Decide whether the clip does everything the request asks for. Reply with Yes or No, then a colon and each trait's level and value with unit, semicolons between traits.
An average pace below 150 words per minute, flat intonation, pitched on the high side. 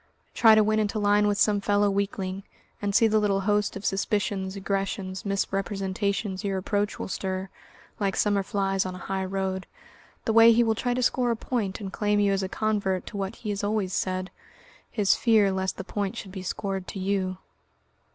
No: average, 200 wpm; narrow, 1.5 semitones; high, 200 Hz